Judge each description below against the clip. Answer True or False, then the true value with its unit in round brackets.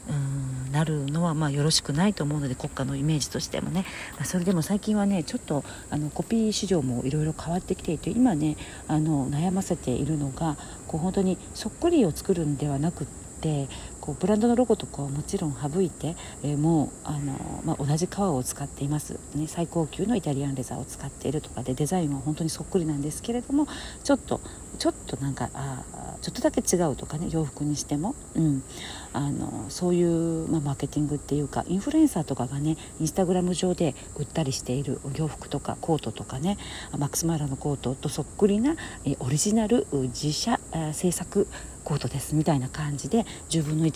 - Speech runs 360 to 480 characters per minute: True (410 characters per minute)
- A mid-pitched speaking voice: True (155 Hz)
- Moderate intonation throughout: True (4.3 semitones)